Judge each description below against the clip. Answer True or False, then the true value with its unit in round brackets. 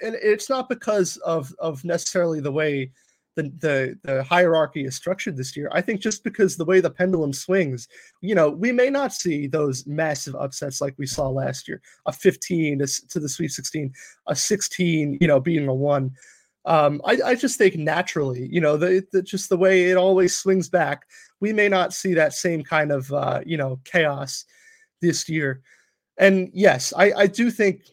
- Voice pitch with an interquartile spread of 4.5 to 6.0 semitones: True (4.8 semitones)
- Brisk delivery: False (195 wpm)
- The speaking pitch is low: False (170 Hz)